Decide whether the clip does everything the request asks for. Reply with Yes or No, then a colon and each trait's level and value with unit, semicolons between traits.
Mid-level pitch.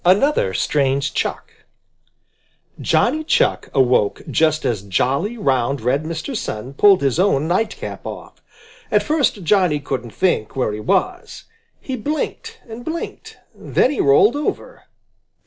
Yes: medium, 165 Hz